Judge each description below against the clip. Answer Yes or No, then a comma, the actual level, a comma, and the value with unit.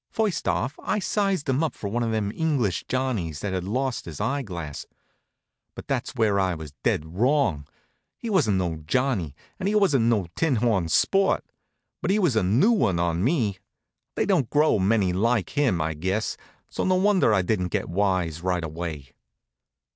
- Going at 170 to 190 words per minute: Yes, average, 175 wpm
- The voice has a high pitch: No, low, 110 Hz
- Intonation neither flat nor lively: No, wide, 8.0 semitones